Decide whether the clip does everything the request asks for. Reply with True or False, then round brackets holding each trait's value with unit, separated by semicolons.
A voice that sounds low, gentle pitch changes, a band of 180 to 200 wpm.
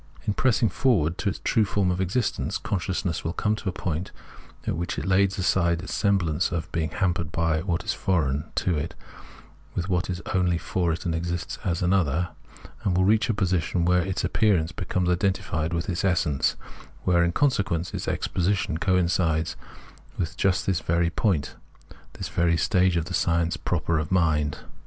True (90 Hz; 2.3 semitones; 185 wpm)